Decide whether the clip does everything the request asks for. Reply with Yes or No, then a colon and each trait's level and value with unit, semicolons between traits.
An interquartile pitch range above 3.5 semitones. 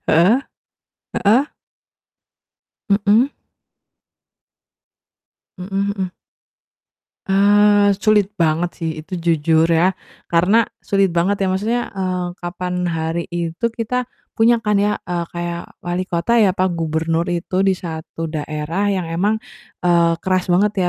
No: average, 3.2 semitones